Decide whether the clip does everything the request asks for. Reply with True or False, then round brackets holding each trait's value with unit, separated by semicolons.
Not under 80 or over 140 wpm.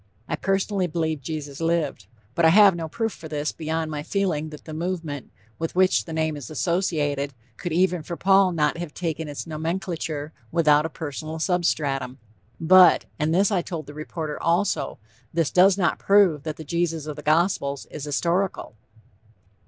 False (175 wpm)